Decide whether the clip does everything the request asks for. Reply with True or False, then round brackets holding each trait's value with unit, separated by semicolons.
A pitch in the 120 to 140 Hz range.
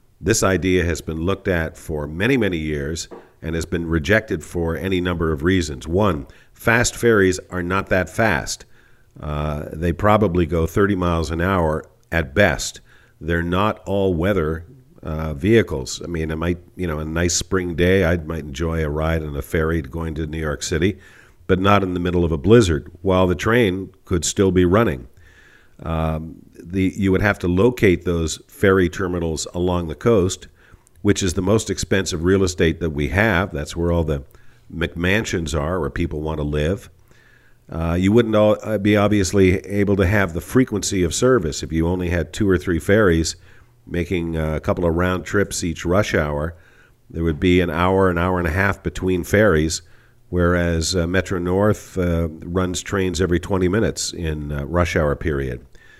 False (90 Hz)